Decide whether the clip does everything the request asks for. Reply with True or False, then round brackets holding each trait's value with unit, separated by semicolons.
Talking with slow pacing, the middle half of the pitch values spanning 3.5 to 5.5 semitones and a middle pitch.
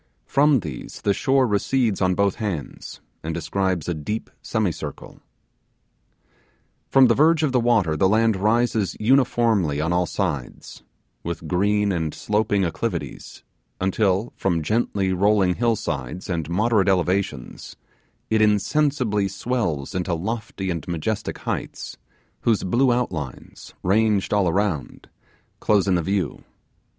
False (130 wpm; 4.3 semitones; 100 Hz)